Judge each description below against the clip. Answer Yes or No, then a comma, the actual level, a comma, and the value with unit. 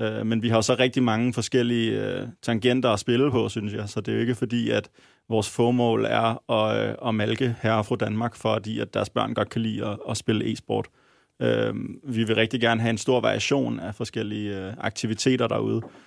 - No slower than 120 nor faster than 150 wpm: No, average, 200 wpm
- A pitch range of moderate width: No, narrow, 2.0 semitones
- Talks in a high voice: No, low, 115 Hz